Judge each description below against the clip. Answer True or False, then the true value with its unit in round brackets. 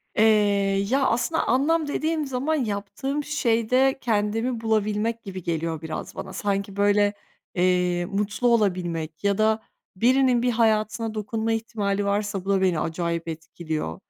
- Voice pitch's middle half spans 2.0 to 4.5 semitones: True (3.5 semitones)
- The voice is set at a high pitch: True (210 Hz)